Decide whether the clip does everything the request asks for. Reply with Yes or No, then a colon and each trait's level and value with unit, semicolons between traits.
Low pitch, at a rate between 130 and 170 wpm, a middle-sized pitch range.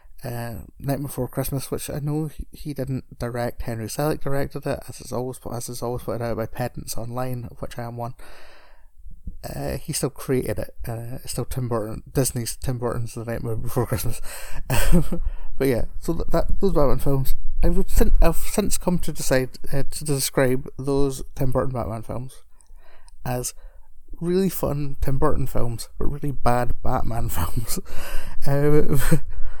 Yes: low, 130 Hz; average, 165 wpm; average, 3.3 semitones